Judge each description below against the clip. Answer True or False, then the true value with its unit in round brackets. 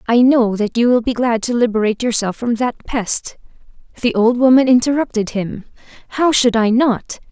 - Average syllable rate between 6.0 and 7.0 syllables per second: False (5.2 syllables/s)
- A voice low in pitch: False (235 Hz)